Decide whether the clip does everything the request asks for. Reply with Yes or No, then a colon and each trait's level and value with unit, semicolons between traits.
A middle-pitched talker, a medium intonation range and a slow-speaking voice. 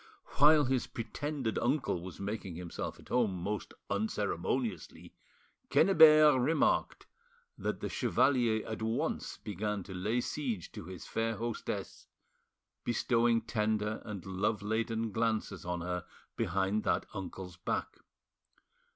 No: low, 110 Hz; average, 3.9 semitones; slow, 120 wpm